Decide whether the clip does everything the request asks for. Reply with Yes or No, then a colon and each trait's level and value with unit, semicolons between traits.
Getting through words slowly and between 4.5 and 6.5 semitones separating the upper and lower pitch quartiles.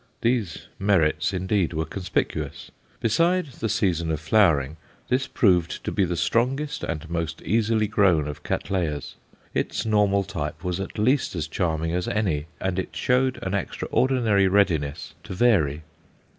No: average, 145 wpm; average, 5.2 semitones